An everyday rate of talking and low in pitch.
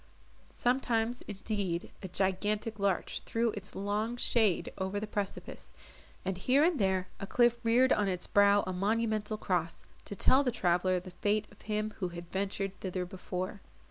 No: average, 165 wpm; high, 205 Hz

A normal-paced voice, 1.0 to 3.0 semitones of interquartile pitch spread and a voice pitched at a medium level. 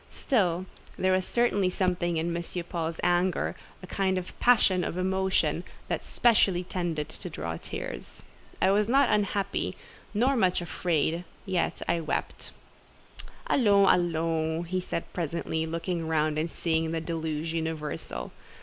No: slow, 130 wpm; average, 2.7 semitones; medium, 175 Hz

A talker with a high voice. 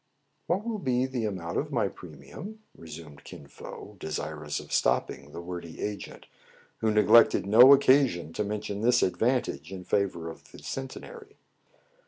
No: low, 105 Hz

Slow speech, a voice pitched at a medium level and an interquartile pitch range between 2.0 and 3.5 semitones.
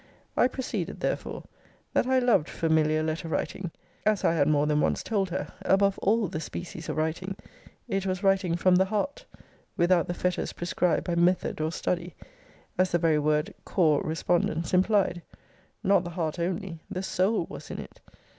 No: average, 175 wpm; medium, 175 Hz; average, 3.1 semitones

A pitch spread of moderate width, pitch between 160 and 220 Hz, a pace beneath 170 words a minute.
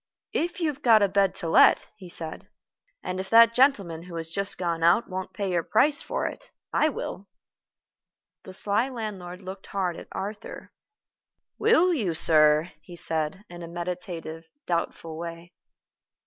Yes: average, 4.1 semitones; medium, 185 Hz; average, 160 wpm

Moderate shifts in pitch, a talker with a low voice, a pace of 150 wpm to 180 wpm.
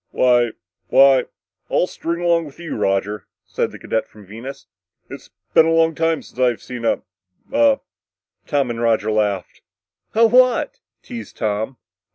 No: wide, 7.0 semitones; low, 130 Hz; average, 160 wpm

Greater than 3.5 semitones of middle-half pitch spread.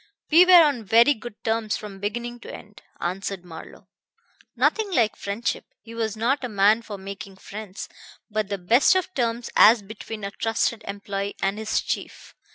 No: average, 3.0 semitones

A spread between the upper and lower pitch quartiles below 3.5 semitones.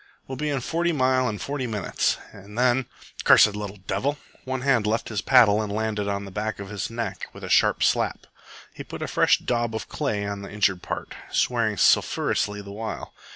No: average, 3.8 semitones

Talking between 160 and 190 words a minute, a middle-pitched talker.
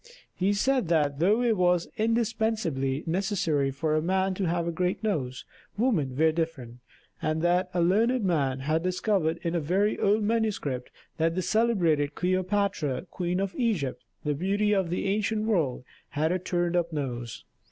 Yes: average, 165 wpm; medium, 175 Hz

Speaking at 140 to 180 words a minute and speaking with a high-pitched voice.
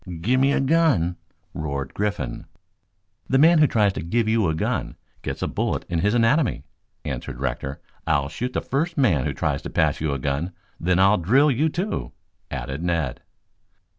No: average, 175 wpm; low, 100 Hz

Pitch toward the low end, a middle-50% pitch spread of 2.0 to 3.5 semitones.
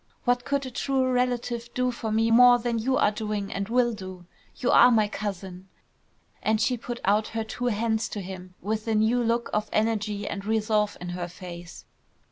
No: high, 220 Hz; average, 3.0 semitones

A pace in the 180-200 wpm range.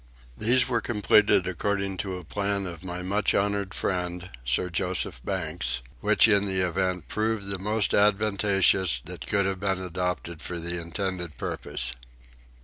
No: average, 150 wpm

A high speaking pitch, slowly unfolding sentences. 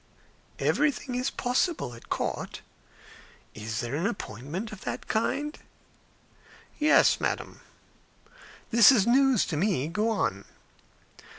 Yes: high, 215 Hz; slow, 110 wpm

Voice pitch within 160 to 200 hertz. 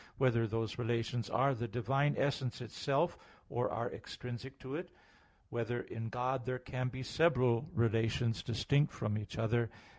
No: low, 120 Hz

